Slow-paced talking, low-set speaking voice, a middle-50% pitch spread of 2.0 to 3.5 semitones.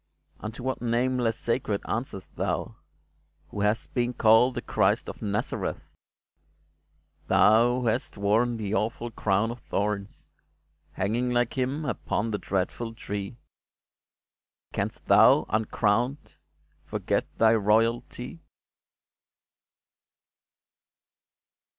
Yes: slow, 100 wpm; low, 115 Hz; narrow, 2.6 semitones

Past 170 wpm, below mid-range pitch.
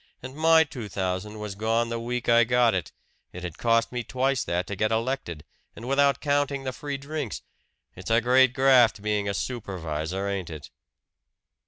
Yes: average, 180 wpm; low, 115 Hz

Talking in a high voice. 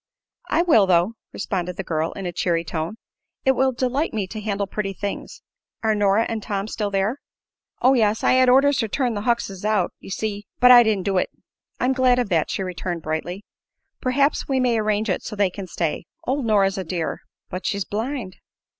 Yes: high, 210 Hz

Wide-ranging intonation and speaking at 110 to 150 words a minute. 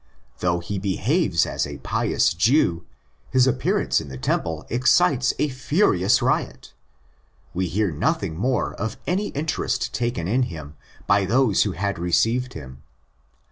Yes: wide, 6.9 semitones; average, 140 wpm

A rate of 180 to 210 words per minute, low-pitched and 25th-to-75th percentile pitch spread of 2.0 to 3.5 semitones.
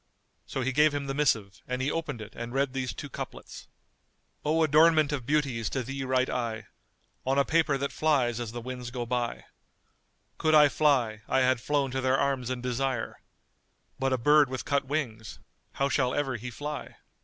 Yes: average, 200 wpm; low, 130 Hz; average, 2.9 semitones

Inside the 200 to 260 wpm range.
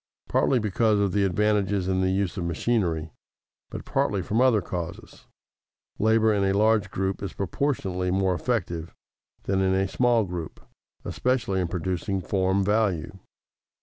No: average, 150 wpm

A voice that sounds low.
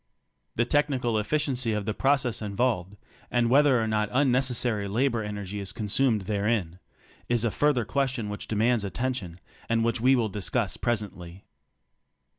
Yes: low, 115 Hz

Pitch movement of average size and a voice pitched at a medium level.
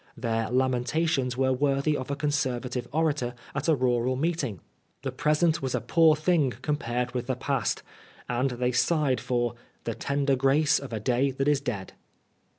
No: average, 3.0 semitones; low, 130 Hz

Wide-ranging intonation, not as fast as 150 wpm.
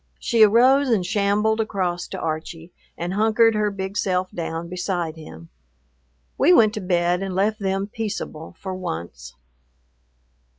No: average, 3.7 semitones; average, 140 wpm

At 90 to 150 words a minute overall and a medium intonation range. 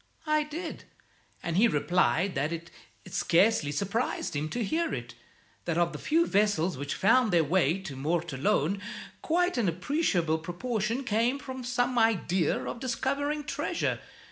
No: average, 145 wpm; wide, 7.4 semitones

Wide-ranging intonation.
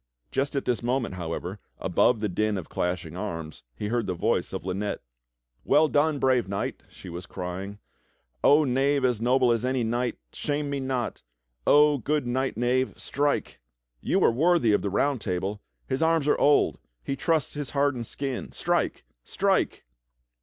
Yes: wide, 6.1 semitones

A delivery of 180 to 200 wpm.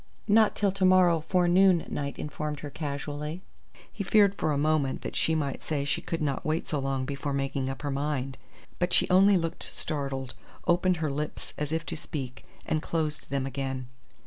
Yes: average, 190 wpm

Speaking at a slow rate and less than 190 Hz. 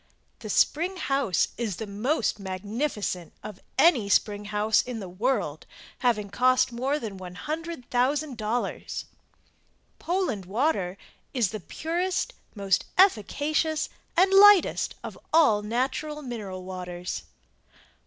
No: slow, 110 wpm; high, 235 Hz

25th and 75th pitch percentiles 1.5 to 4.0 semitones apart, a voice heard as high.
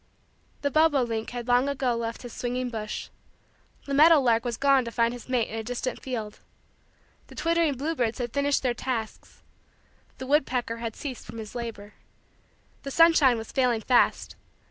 Yes: average, 3.1 semitones; high, 245 Hz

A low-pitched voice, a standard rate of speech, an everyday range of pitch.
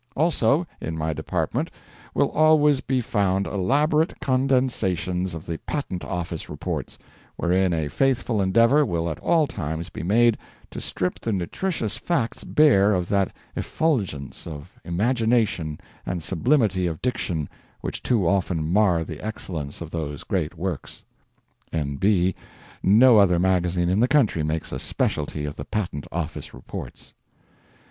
No: very low, 95 Hz; average, 145 wpm; wide, 6.5 semitones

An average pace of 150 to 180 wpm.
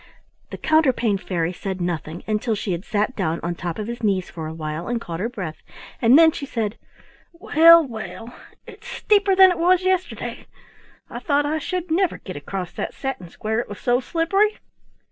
No: average, 190 wpm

